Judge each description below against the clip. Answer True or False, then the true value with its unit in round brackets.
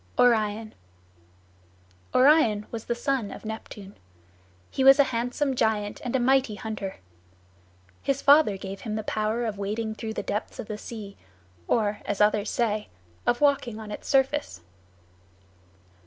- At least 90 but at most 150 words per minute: True (145 wpm)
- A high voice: True (220 Hz)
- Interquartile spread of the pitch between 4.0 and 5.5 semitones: False (3.5 semitones)